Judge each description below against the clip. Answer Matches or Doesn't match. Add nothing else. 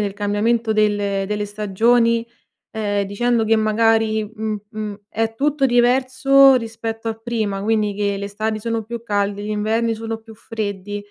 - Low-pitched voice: Doesn't match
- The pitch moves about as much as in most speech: Doesn't match